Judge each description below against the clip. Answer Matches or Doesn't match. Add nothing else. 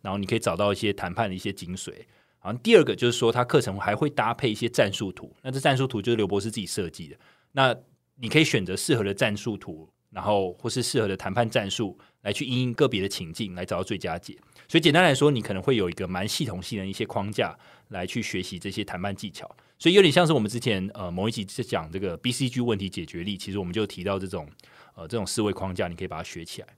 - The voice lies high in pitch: Doesn't match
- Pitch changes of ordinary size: Matches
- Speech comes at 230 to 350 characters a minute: Doesn't match